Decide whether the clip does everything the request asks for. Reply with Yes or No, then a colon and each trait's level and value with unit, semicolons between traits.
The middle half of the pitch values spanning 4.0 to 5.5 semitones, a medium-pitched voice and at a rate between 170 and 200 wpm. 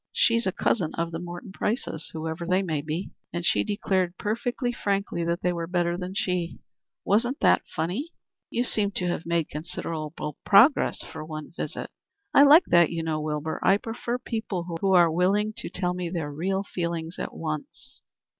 No: average, 3.5 semitones; medium, 175 Hz; average, 180 wpm